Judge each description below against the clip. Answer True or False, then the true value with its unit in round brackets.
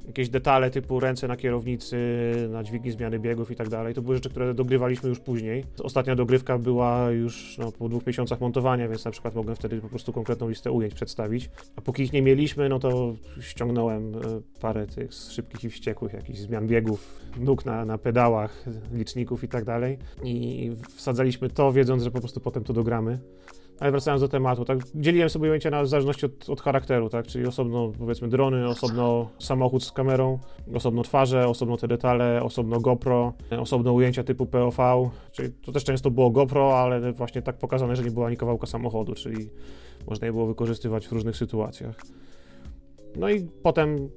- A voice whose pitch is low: True (120 Hz)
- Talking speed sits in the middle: False (180 wpm)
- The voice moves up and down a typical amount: False (2.0 semitones)